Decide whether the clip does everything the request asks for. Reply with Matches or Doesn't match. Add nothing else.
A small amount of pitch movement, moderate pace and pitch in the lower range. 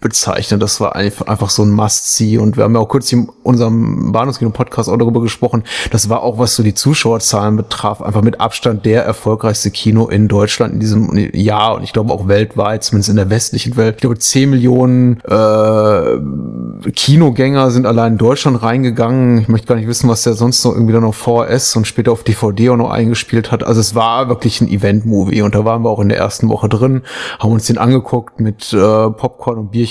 Doesn't match